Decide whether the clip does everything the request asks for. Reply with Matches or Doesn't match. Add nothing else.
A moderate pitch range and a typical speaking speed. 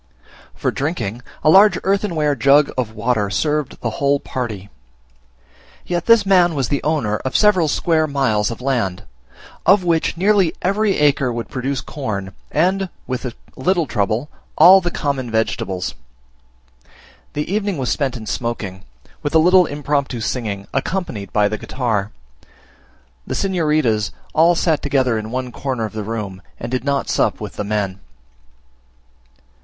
Doesn't match